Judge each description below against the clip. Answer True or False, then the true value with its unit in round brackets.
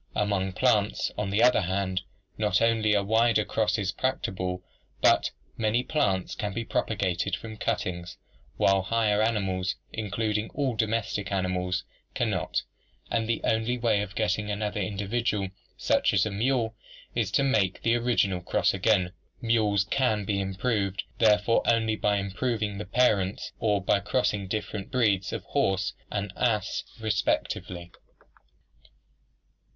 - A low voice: True (105 Hz)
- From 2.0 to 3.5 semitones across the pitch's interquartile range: True (2.7 semitones)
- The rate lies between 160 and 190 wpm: False (140 wpm)